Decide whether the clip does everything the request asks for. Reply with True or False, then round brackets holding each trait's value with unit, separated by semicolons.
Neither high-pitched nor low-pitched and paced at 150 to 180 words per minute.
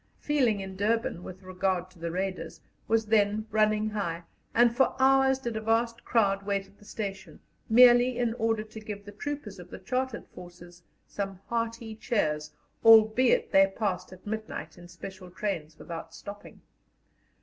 False (210 Hz; 160 wpm)